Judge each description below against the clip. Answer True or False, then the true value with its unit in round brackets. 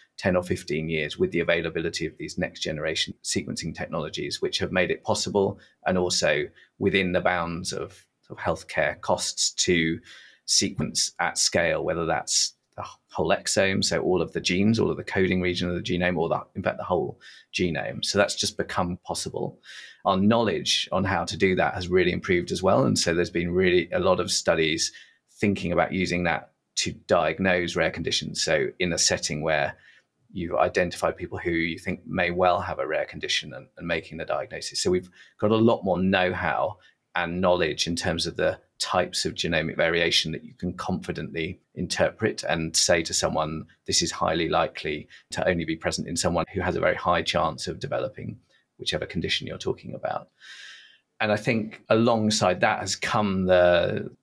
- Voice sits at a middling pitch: False (90 Hz)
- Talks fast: False (190 wpm)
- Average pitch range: False (2.1 semitones)